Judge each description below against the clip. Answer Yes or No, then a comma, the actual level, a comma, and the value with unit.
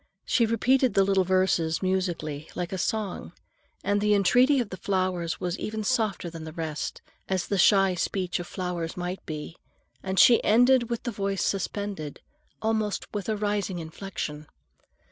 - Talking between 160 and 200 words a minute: Yes, average, 165 wpm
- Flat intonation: No, average, 3.3 semitones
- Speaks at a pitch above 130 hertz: Yes, high, 190 Hz